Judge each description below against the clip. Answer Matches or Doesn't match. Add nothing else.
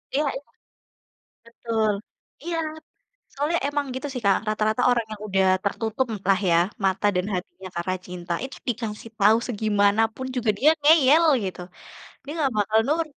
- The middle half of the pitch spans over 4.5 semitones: Matches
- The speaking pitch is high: Matches